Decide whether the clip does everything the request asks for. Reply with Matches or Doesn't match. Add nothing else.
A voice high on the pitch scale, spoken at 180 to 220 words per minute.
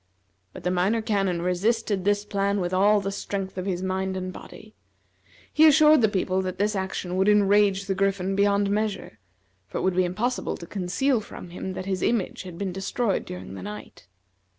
Matches